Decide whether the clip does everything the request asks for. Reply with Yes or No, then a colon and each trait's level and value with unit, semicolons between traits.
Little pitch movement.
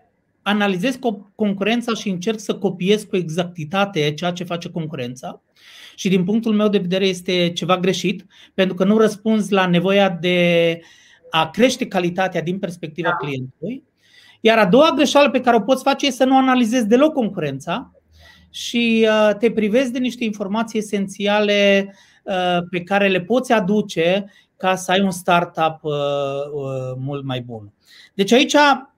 No: average, 4.3 semitones